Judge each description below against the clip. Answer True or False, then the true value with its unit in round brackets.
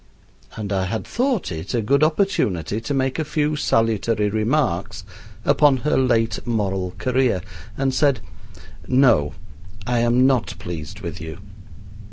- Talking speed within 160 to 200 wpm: False (140 wpm)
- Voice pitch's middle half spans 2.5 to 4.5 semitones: False (5.1 semitones)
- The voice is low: True (120 Hz)